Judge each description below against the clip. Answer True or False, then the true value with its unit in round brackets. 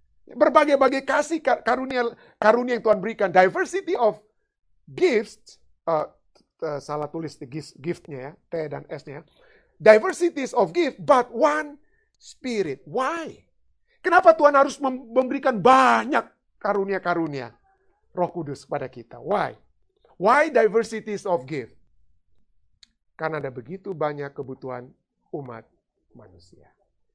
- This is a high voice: True (225 Hz)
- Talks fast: False (110 wpm)